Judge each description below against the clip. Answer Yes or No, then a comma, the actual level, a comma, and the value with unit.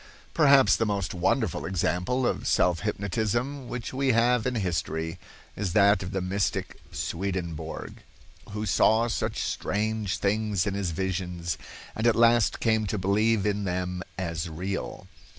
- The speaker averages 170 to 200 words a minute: No, average, 145 wpm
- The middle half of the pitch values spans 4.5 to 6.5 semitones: No, average, 3.6 semitones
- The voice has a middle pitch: No, low, 100 Hz